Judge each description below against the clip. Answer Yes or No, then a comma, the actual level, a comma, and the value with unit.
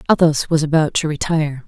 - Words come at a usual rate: Yes, average, 180 wpm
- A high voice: No, medium, 155 Hz